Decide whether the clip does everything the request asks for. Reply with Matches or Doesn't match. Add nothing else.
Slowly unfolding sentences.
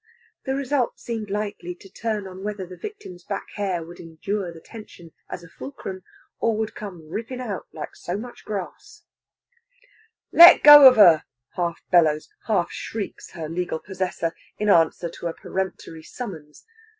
Doesn't match